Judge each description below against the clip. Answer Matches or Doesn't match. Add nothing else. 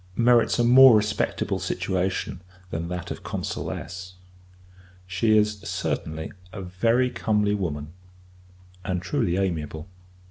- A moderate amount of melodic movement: Matches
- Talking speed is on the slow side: Matches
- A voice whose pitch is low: Matches